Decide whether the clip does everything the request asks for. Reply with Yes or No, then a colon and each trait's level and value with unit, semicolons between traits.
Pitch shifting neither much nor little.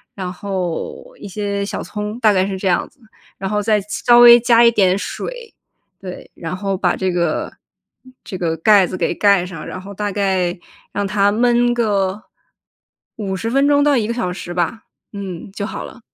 Yes: average, 3.1 semitones